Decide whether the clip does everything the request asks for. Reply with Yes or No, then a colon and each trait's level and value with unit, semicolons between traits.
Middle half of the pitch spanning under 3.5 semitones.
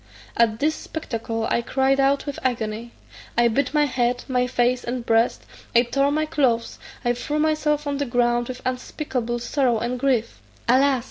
Yes: average, 2.9 semitones